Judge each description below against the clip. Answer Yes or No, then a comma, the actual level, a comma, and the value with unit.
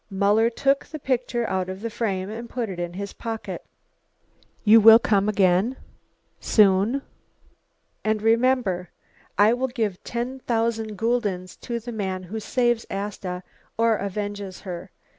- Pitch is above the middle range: Yes, high, 215 Hz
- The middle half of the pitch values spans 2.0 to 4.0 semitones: Yes, average, 3.4 semitones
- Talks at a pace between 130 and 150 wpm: Yes, average, 140 wpm